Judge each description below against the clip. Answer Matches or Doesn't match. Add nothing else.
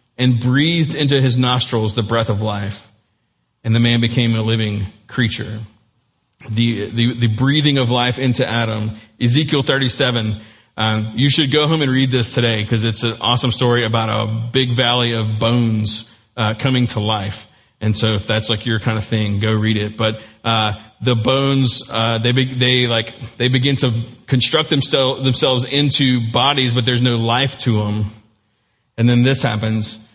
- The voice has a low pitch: Matches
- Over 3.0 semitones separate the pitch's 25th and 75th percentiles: Doesn't match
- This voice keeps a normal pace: Matches